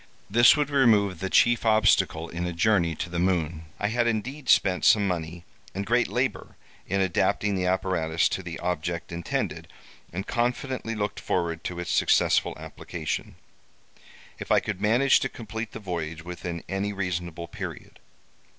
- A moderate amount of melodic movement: Yes, average, 4.2 semitones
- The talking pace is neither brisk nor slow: Yes, average, 160 wpm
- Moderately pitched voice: No, very low, 95 Hz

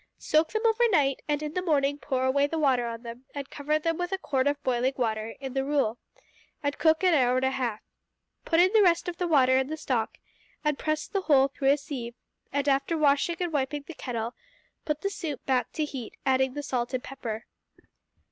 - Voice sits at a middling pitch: No, very high, 280 Hz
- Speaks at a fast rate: Yes, fast, 225 wpm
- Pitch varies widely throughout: No, average, 3.2 semitones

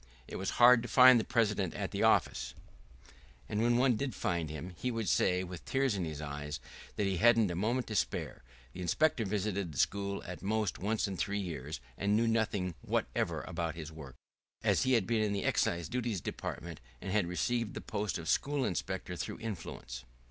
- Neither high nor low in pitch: No, low, 100 Hz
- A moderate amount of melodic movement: Yes, average, 4.9 semitones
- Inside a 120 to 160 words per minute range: No, average, 200 wpm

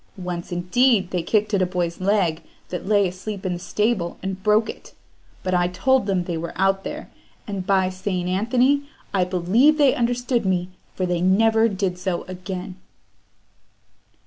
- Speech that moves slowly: No, average, 170 wpm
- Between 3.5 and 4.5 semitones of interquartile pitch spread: No, average, 3.1 semitones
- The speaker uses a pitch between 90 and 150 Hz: No, high, 190 Hz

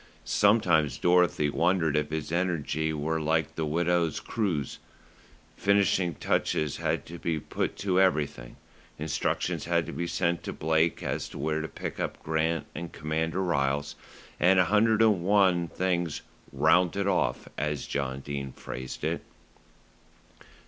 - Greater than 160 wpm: No, average, 140 wpm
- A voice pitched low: Yes, very low, 80 Hz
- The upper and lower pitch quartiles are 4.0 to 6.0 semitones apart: No, average, 2.9 semitones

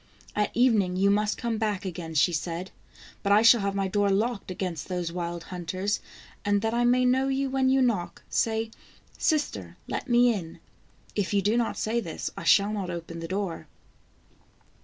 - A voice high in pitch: Yes, high, 205 Hz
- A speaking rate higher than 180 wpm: Yes, average, 195 wpm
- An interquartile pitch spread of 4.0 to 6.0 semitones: Yes, average, 4.4 semitones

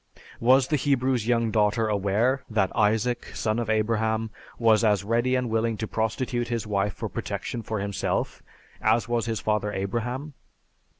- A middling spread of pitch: No, narrow, 2.1 semitones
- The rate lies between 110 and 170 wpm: Yes, average, 160 wpm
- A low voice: Yes, low, 115 Hz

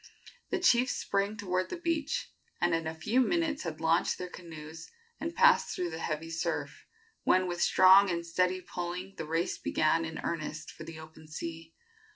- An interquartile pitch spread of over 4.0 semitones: No, average, 3.5 semitones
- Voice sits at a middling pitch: Yes, medium, 175 Hz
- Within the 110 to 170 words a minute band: No, average, 180 wpm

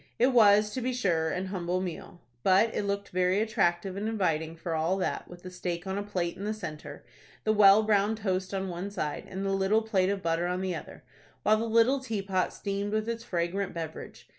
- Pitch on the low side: No, high, 195 Hz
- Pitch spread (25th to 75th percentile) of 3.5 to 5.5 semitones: No, average, 3.1 semitones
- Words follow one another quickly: Yes, fast, 215 wpm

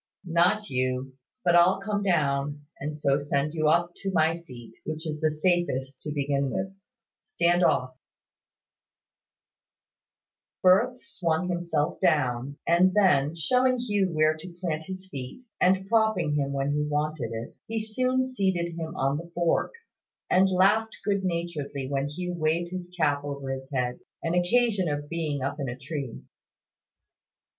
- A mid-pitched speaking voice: Yes, medium, 165 Hz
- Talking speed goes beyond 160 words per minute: No, average, 150 wpm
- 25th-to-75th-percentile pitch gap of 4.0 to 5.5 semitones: Yes, average, 4.6 semitones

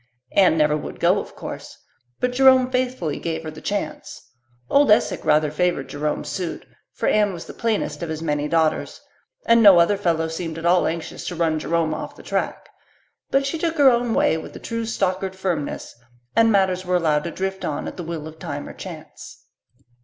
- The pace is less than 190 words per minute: No, average, 200 wpm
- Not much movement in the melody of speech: No, average, 5.3 semitones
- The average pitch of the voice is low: No, medium, 180 Hz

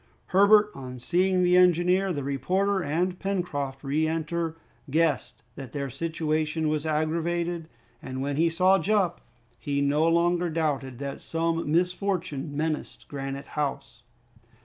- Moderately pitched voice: Yes, medium, 160 Hz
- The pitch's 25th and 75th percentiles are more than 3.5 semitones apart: Yes, average, 3.9 semitones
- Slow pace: Yes, slow, 130 wpm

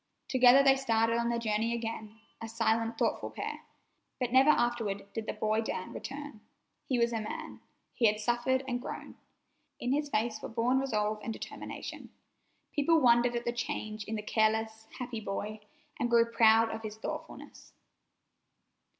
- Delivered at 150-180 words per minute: Yes, average, 165 wpm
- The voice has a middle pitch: No, high, 230 Hz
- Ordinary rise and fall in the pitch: No, narrow, 1.9 semitones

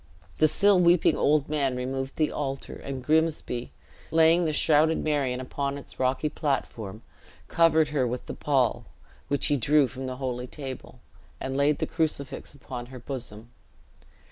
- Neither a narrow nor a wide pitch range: Yes, average, 3.1 semitones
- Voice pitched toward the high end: No, medium, 140 Hz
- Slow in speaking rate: No, average, 155 wpm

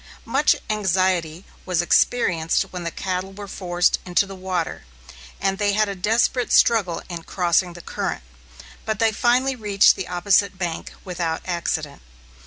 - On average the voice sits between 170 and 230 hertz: Yes, medium, 185 Hz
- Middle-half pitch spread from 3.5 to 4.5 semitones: No, average, 3.0 semitones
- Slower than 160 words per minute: Yes, average, 150 wpm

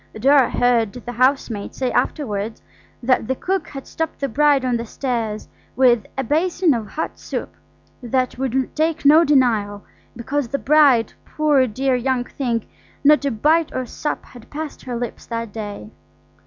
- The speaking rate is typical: Yes, average, 165 wpm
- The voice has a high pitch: Yes, very high, 255 Hz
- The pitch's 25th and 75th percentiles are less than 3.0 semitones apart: No, average, 3.8 semitones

